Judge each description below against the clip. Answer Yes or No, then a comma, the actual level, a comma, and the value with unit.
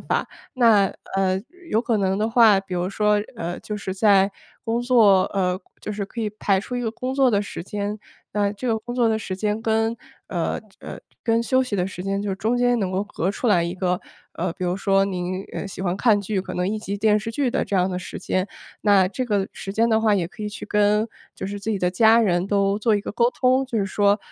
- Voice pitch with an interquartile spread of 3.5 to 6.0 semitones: No, average, 2.7 semitones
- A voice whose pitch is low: No, high, 205 Hz